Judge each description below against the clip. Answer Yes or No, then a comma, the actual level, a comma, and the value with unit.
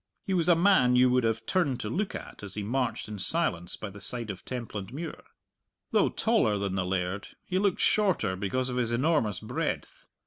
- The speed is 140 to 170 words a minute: No, average, 200 wpm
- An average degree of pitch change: No, wide, 8.1 semitones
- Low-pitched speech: Yes, low, 120 Hz